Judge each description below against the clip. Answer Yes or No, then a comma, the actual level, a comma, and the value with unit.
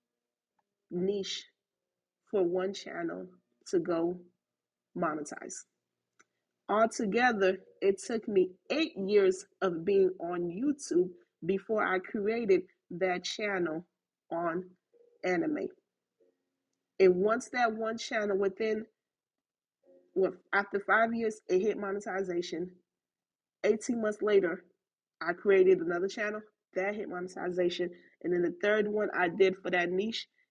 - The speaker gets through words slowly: Yes, slow, 115 wpm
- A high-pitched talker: Yes, high, 195 Hz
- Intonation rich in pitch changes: No, average, 3.7 semitones